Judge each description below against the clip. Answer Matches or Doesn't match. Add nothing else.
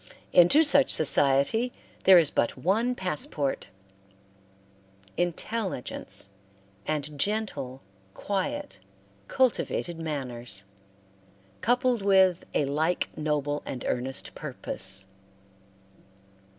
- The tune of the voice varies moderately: Doesn't match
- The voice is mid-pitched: Matches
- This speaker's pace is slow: Matches